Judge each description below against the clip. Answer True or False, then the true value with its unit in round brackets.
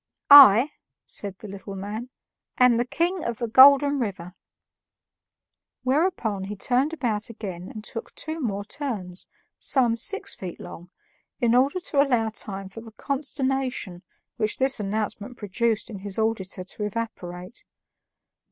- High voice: True (225 Hz)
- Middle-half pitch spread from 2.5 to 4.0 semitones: False (4.9 semitones)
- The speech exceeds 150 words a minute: False (140 wpm)